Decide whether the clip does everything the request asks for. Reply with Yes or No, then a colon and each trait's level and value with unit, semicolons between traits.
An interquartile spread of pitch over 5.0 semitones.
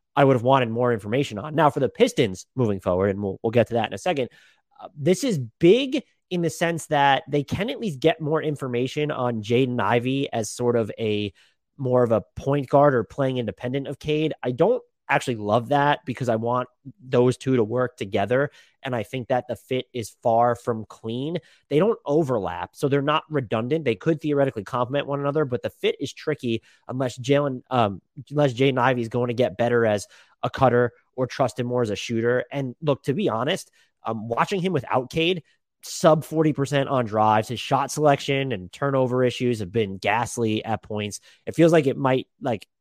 No: average, 3.4 semitones